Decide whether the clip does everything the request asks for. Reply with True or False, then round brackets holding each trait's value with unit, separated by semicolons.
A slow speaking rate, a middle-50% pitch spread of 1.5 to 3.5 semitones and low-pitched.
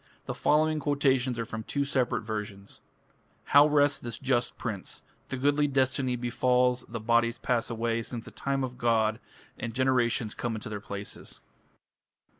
False (160 wpm; 2.8 semitones; 120 Hz)